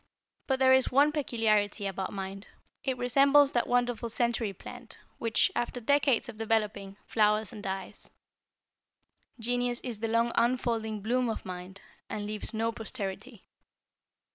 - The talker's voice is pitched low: No, high, 230 Hz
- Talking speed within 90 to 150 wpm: Yes, average, 140 wpm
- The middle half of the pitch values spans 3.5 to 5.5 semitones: No, average, 2.9 semitones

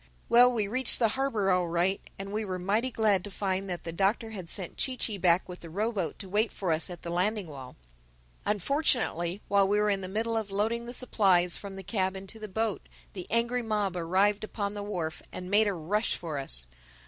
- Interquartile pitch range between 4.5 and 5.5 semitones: No, average, 3.3 semitones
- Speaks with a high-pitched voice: Yes, high, 200 Hz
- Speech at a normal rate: No, fast, 225 wpm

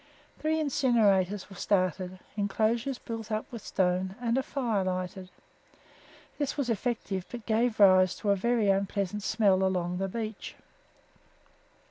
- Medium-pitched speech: No, high, 205 Hz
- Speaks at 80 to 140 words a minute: Yes, slow, 135 wpm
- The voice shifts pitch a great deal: No, average, 3.9 semitones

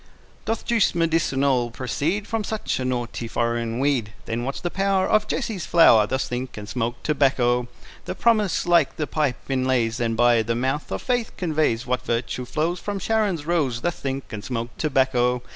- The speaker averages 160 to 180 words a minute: Yes, average, 175 wpm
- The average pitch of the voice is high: No, low, 135 Hz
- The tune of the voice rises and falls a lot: Yes, wide, 6.1 semitones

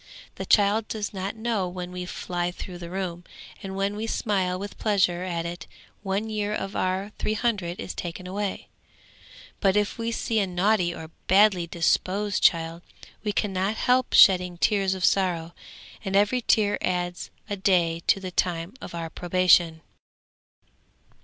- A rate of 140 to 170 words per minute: Yes, average, 160 wpm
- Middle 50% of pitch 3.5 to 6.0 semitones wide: No, narrow, 2.6 semitones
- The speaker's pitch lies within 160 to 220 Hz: Yes, high, 190 Hz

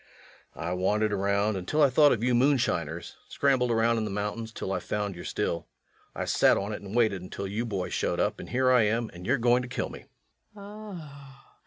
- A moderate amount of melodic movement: Yes, average, 4.0 semitones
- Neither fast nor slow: No, fast, 210 wpm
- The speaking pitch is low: Yes, low, 110 Hz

